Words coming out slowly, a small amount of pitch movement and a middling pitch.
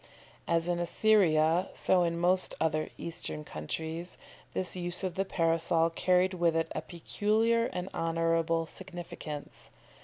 Yes: slow, 130 wpm; narrow, 1.9 semitones; medium, 170 Hz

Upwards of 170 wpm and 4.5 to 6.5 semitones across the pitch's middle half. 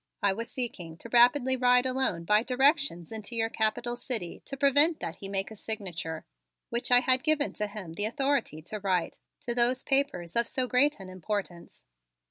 Yes: average, 185 wpm; average, 5.0 semitones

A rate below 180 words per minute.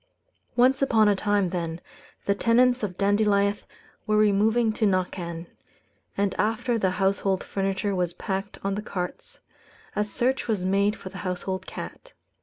Yes: average, 150 wpm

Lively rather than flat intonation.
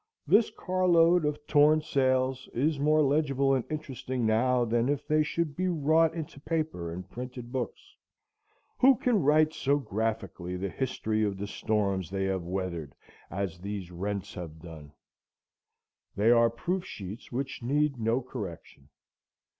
Yes: wide, 7.2 semitones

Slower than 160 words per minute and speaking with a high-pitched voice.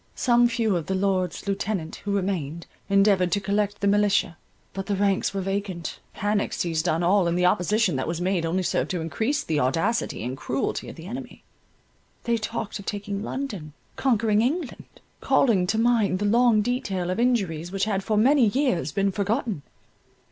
No: average, 175 wpm; high, 200 Hz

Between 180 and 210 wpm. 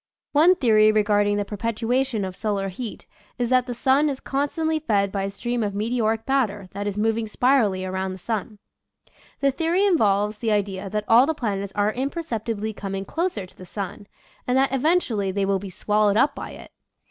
Yes: average, 190 wpm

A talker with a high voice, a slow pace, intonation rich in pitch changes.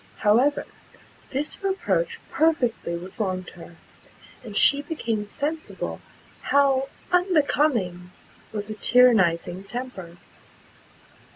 Yes: high, 245 Hz; slow, 85 wpm; wide, 7.4 semitones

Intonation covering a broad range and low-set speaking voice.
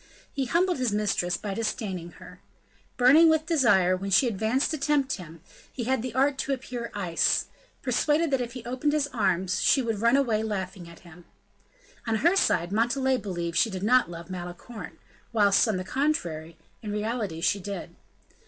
No: wide, 6.1 semitones; high, 220 Hz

